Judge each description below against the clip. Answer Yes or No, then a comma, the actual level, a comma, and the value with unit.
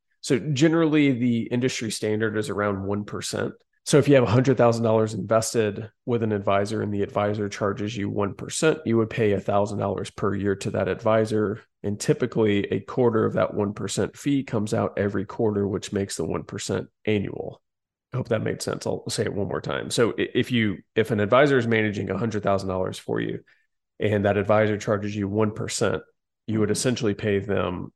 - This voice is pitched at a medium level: No, low, 105 Hz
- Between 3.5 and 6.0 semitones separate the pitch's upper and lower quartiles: No, narrow, 2.4 semitones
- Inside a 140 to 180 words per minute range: Yes, average, 175 wpm